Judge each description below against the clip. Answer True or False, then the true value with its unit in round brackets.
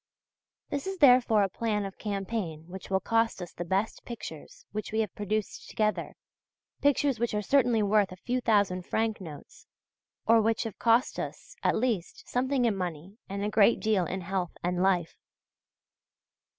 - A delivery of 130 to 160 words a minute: False (170 wpm)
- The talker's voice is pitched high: True (210 Hz)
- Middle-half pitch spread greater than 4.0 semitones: False (3.4 semitones)